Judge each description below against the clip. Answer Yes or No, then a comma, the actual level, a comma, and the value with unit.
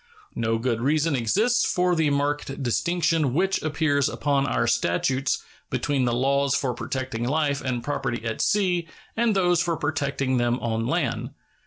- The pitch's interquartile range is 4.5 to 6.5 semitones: Yes, average, 4.8 semitones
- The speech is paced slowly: No, average, 155 wpm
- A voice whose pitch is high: No, medium, 140 Hz